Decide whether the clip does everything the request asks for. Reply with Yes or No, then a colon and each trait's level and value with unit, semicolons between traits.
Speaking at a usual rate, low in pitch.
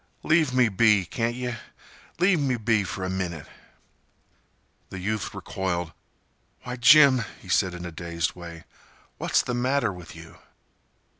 Yes: average, 145 wpm; low, 105 Hz